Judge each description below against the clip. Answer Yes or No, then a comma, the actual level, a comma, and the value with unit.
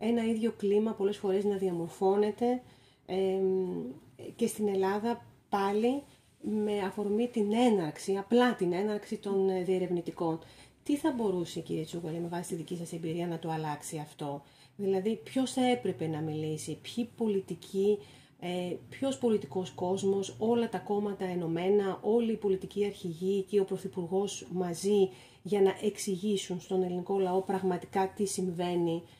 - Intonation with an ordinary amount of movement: Yes, average, 3.0 semitones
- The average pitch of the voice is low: No, high, 190 Hz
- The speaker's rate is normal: Yes, average, 145 wpm